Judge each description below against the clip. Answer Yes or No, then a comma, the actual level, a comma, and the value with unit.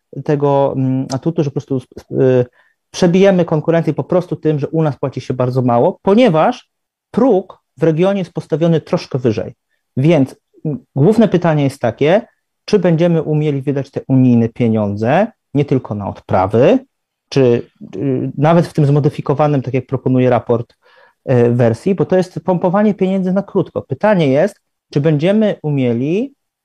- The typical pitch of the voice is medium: Yes, medium, 150 Hz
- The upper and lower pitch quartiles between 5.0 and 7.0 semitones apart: Yes, wide, 5.5 semitones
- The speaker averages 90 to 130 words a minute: No, average, 145 wpm